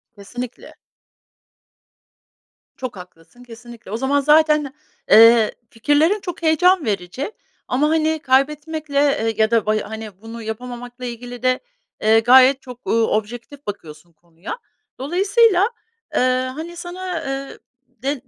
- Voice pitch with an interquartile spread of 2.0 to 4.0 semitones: No, average, 5.3 semitones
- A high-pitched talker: Yes, very high, 250 Hz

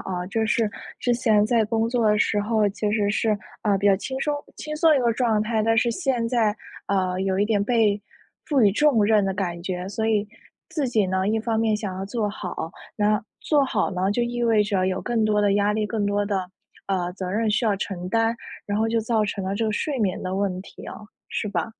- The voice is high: Yes, high, 210 Hz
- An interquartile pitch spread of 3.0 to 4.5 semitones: No, narrow, 2.5 semitones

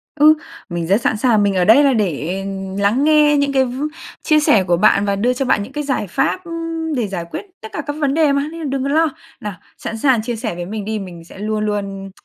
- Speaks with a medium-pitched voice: No, high, 225 Hz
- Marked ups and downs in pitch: Yes, wide, 6.3 semitones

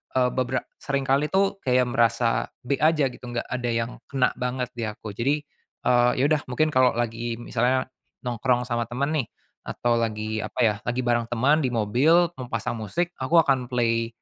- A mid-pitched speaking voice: No, low, 125 Hz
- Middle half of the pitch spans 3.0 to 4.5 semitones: No, narrow, 2.5 semitones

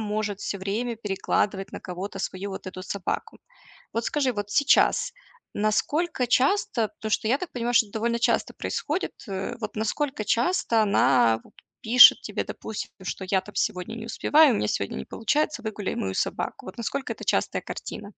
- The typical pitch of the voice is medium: No, high, 220 Hz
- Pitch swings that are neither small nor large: Yes, average, 3.8 semitones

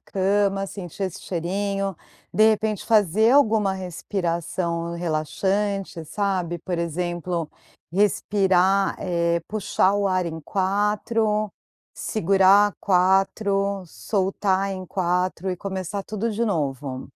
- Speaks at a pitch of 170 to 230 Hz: Yes, high, 190 Hz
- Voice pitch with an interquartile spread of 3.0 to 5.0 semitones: No, narrow, 2.6 semitones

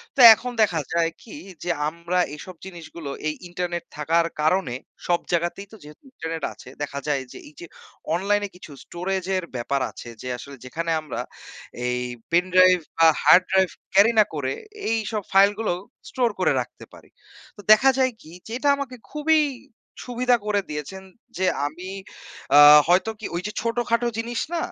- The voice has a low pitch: No, medium, 180 Hz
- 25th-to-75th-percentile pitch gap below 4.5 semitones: No, average, 5.0 semitones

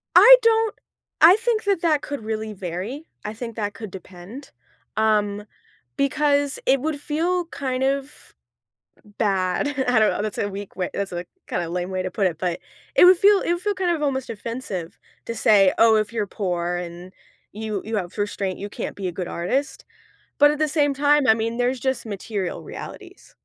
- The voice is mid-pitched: No, high, 225 Hz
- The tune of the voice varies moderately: No, wide, 6.9 semitones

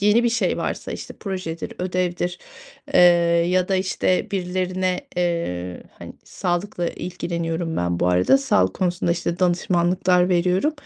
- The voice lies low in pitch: No, medium, 180 Hz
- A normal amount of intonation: No, narrow, 1.5 semitones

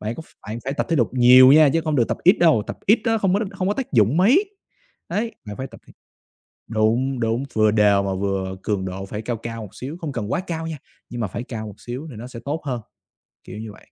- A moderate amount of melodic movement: No, wide, 7.0 semitones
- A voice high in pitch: No, low, 120 Hz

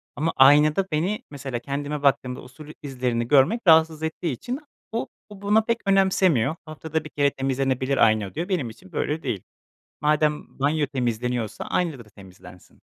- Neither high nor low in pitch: Yes, medium, 145 Hz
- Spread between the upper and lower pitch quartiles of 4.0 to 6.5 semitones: Yes, average, 4.3 semitones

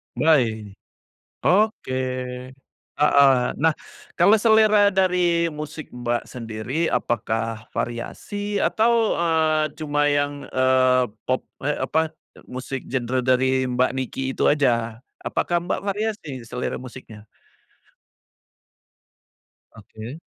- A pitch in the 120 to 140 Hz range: Yes, low, 135 Hz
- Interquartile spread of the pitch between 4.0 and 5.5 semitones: Yes, average, 4.6 semitones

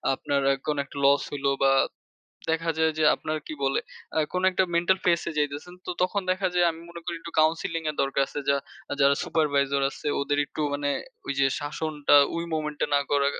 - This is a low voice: No, medium, 150 Hz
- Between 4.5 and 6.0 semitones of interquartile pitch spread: No, average, 2.9 semitones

